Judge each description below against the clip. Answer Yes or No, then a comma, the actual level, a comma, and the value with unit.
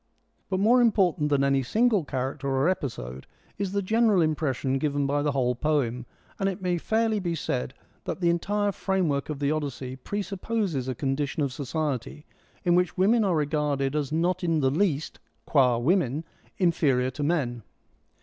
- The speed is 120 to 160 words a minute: No, average, 170 wpm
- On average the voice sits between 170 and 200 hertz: No, medium, 150 Hz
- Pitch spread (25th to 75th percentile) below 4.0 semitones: No, wide, 5.4 semitones